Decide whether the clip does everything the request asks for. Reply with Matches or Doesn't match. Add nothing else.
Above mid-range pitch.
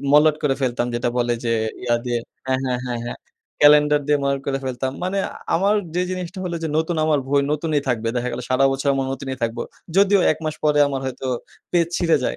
Doesn't match